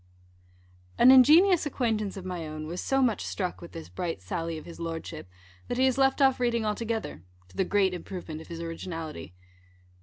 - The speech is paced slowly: No, average, 190 wpm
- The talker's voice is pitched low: No, medium, 185 Hz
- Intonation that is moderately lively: No, wide, 6.8 semitones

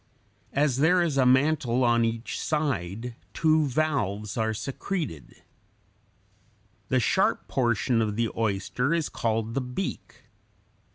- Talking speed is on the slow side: Yes, slow, 120 wpm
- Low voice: Yes, low, 125 Hz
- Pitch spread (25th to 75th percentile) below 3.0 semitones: No, average, 4.7 semitones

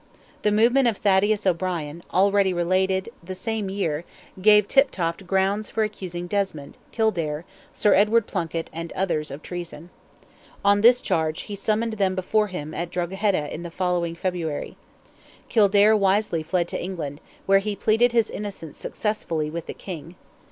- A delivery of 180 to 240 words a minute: No, average, 150 wpm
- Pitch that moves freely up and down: No, average, 3.7 semitones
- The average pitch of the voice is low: No, high, 190 Hz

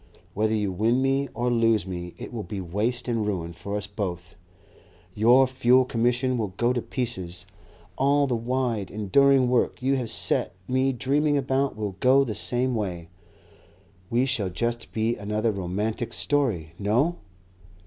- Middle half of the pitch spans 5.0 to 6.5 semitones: No, average, 4.0 semitones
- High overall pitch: No, low, 115 Hz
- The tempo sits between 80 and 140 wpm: No, average, 160 wpm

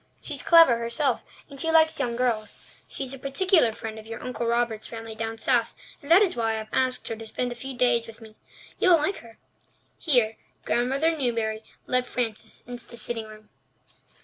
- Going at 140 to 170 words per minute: No, average, 200 wpm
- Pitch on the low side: No, high, 240 Hz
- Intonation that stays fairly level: No, average, 3.2 semitones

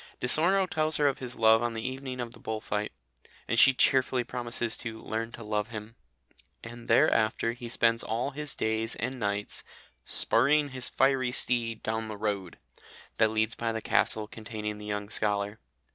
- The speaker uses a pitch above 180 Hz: No, low, 115 Hz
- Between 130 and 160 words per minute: No, average, 180 wpm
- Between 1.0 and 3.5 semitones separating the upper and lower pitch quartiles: Yes, narrow, 2.6 semitones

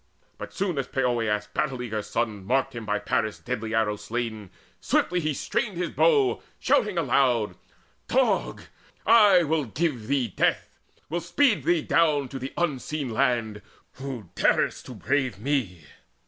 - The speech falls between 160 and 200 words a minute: No, average, 150 wpm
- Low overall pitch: Yes, low, 130 Hz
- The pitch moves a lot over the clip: Yes, wide, 6.2 semitones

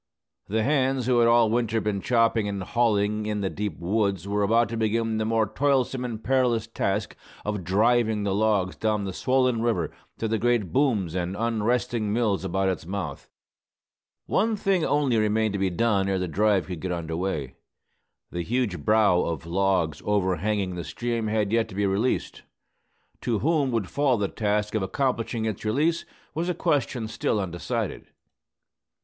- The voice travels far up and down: No, average, 3.4 semitones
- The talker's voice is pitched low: Yes, low, 110 Hz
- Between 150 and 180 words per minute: Yes, average, 175 wpm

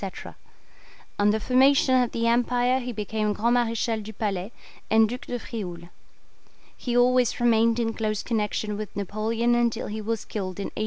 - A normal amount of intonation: No, narrow, 2.3 semitones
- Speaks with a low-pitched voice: No, high, 225 Hz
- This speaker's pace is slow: No, average, 165 wpm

